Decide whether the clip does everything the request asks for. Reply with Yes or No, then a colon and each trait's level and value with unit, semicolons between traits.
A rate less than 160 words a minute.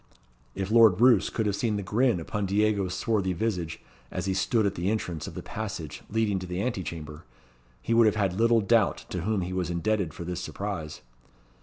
No: fast, 205 wpm